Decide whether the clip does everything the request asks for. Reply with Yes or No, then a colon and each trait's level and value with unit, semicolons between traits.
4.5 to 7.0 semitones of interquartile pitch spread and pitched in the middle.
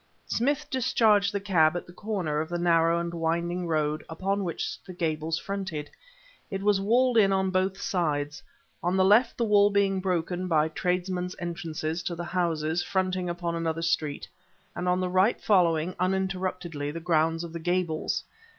No: average, 2.7 semitones; medium, 175 Hz